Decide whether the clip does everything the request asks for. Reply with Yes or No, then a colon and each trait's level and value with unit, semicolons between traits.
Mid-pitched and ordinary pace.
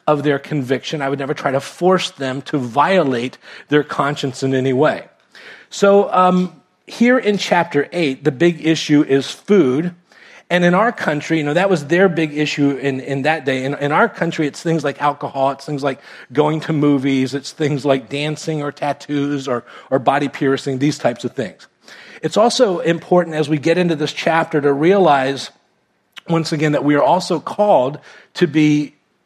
Yes: medium, 150 Hz; average, 185 wpm